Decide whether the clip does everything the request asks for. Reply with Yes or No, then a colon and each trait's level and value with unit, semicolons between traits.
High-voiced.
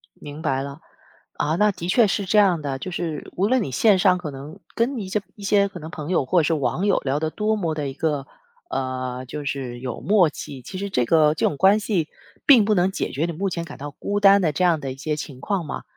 No: medium, 165 Hz